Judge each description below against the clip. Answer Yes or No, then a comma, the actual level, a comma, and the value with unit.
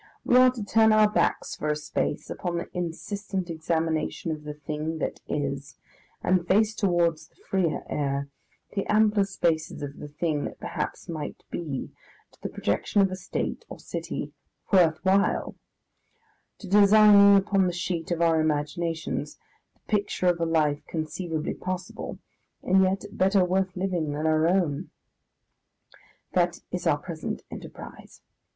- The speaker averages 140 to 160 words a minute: Yes, average, 150 wpm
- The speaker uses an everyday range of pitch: Yes, average, 3.7 semitones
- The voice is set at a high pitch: No, medium, 175 Hz